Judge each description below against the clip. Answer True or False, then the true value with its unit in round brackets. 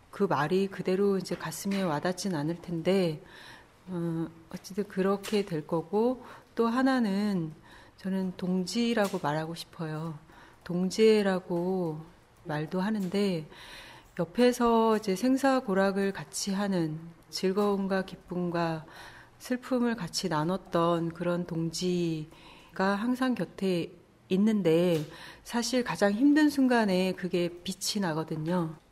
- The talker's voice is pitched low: False (185 Hz)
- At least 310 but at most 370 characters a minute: False (230 characters per minute)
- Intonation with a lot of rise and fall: False (3.3 semitones)